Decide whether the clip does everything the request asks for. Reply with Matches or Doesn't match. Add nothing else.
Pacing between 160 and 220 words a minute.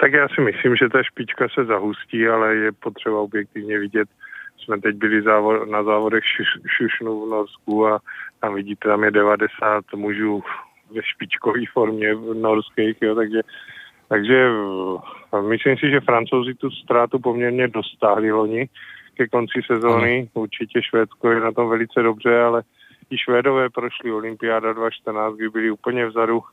Doesn't match